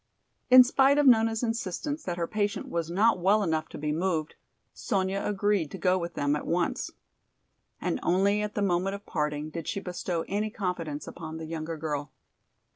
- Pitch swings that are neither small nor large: Yes, average, 4.3 semitones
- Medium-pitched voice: Yes, medium, 180 Hz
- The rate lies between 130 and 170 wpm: No, average, 185 wpm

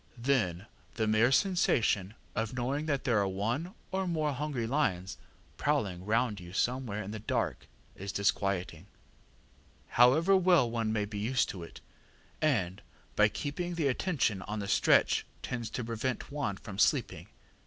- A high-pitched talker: No, low, 115 Hz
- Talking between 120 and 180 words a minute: Yes, average, 155 wpm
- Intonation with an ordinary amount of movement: No, wide, 5.8 semitones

